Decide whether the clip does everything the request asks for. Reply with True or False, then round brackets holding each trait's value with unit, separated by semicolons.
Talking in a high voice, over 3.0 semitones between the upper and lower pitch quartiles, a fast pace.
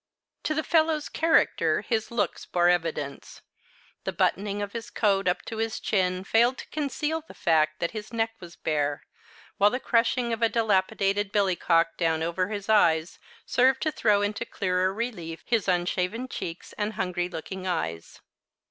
False (200 Hz; 4.7 semitones; 165 wpm)